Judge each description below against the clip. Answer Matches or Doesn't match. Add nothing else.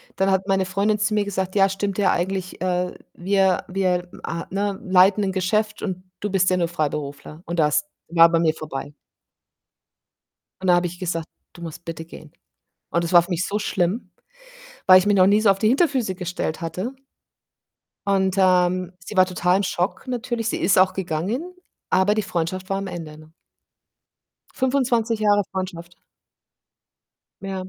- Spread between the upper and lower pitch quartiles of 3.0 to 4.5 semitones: Doesn't match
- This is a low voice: Doesn't match